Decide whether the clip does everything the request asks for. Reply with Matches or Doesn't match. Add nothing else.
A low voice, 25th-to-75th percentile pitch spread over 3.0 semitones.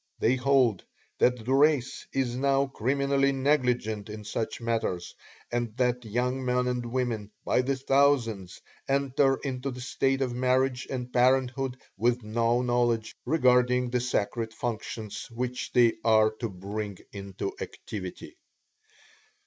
Doesn't match